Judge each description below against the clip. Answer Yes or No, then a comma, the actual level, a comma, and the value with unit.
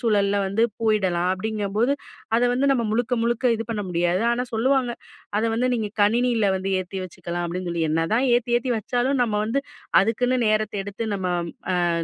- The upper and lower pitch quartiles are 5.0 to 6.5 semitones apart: No, average, 3.9 semitones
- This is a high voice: Yes, high, 220 Hz